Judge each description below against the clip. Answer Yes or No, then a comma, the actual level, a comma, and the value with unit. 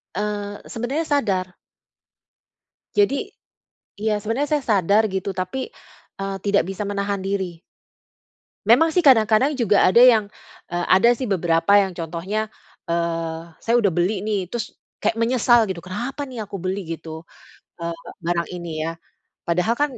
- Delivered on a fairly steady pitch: No, average, 4.3 semitones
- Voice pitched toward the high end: Yes, high, 200 Hz